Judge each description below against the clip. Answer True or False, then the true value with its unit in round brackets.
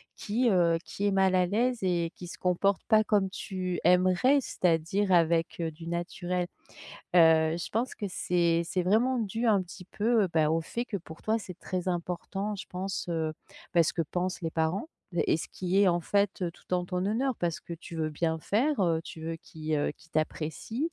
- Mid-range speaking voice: True (180 Hz)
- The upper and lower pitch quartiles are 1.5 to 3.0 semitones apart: False (3.4 semitones)